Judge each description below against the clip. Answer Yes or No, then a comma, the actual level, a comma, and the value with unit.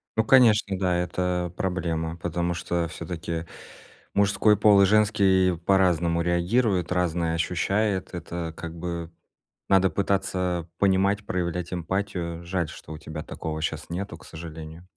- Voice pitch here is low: Yes, very low, 90 Hz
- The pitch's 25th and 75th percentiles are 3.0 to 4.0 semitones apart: No, narrow, 2.4 semitones